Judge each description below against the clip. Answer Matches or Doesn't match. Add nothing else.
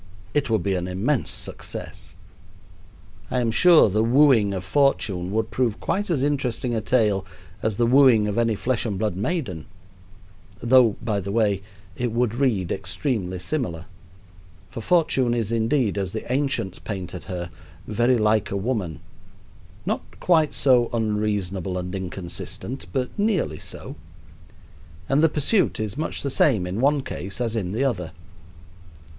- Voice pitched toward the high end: Doesn't match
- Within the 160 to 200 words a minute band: Doesn't match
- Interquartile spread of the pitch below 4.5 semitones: Doesn't match